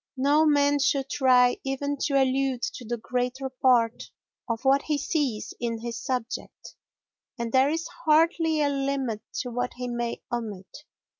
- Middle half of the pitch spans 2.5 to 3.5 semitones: Yes, average, 2.9 semitones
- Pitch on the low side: No, very high, 260 Hz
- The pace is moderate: Yes, average, 155 wpm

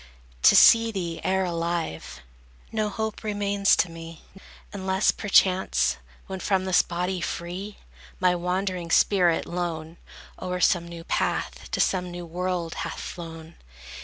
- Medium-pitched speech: Yes, medium, 180 Hz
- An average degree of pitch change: No, narrow, 2.1 semitones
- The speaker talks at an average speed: No, slow, 130 wpm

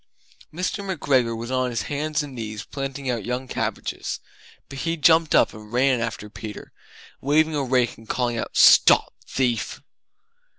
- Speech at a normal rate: Yes, average, 160 wpm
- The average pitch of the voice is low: Yes, low, 130 Hz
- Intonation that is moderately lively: Yes, average, 3.8 semitones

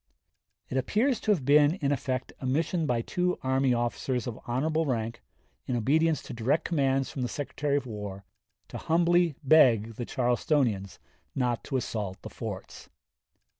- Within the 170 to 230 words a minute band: No, average, 160 wpm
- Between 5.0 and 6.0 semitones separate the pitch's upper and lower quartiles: No, average, 4.3 semitones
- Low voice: Yes, low, 130 Hz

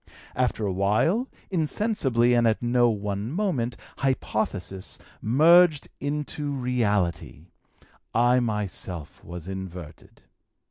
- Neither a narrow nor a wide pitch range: No, wide, 6.3 semitones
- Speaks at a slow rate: Yes, slow, 95 wpm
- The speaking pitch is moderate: No, low, 120 Hz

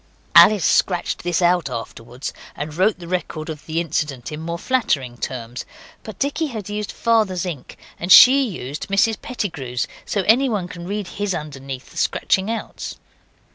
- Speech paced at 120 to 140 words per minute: No, average, 160 wpm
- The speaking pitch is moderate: Yes, medium, 175 Hz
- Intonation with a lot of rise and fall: Yes, wide, 6.0 semitones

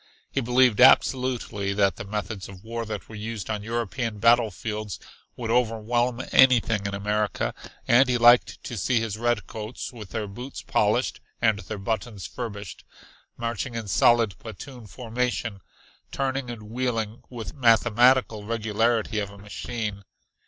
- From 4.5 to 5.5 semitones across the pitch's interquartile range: No, narrow, 2.5 semitones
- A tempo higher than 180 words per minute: No, average, 145 wpm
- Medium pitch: No, low, 115 Hz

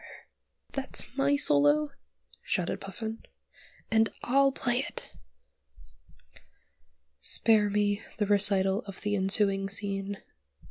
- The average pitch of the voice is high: Yes, high, 205 Hz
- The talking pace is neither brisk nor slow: No, slow, 95 wpm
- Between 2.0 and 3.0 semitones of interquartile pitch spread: Yes, narrow, 2.4 semitones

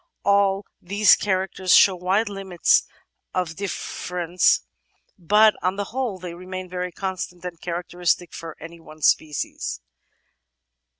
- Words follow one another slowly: Yes, slow, 120 wpm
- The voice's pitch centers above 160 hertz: Yes, medium, 185 Hz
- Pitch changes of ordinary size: No, narrow, 2.0 semitones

